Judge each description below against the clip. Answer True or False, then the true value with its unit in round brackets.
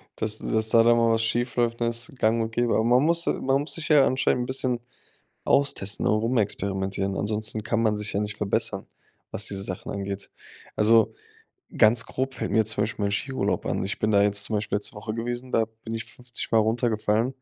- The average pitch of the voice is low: True (115 Hz)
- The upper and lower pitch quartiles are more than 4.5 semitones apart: False (2.6 semitones)